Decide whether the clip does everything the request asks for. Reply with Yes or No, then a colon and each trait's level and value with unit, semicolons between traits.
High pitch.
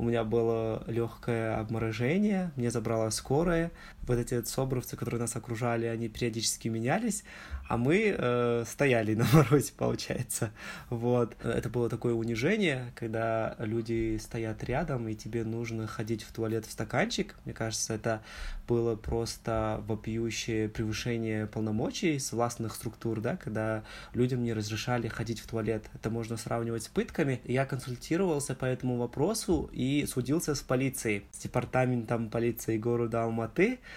No: low, 115 Hz